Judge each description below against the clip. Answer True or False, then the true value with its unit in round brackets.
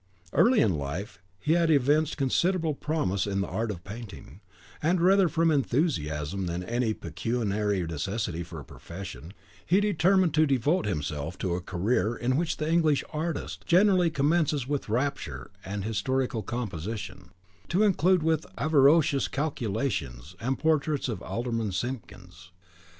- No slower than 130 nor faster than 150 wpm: True (140 wpm)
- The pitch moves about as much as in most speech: False (8.4 semitones)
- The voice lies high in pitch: False (125 Hz)